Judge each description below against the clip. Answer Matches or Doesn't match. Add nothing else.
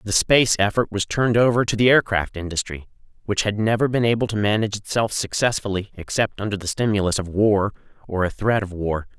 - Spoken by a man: Matches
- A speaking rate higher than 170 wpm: Matches